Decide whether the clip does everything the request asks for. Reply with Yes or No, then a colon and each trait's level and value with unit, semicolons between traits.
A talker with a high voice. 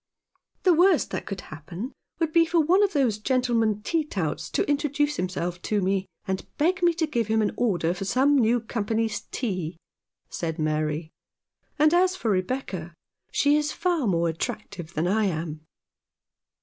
Yes: high, 220 Hz